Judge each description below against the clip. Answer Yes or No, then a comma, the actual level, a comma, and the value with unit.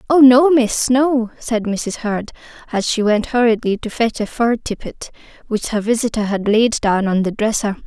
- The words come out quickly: No, average, 190 wpm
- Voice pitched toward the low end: No, high, 225 Hz